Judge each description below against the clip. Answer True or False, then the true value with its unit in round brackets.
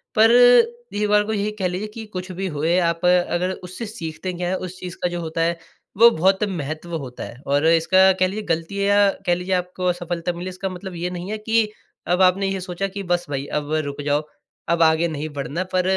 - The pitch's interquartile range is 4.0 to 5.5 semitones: False (2.8 semitones)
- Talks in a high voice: False (180 Hz)